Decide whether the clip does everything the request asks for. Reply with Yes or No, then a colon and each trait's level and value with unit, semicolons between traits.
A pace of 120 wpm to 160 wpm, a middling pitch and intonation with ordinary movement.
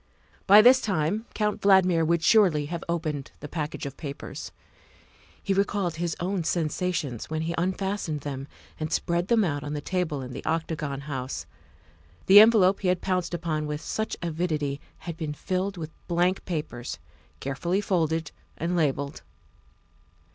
Yes: average, 155 wpm; medium, 170 Hz; average, 3.8 semitones